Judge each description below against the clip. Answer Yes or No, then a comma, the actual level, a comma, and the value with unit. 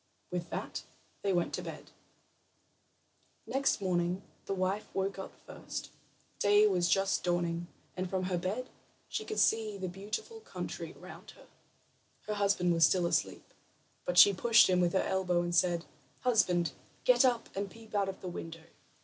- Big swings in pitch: No, average, 2.8 semitones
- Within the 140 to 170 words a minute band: Yes, average, 165 wpm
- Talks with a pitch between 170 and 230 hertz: Yes, high, 190 Hz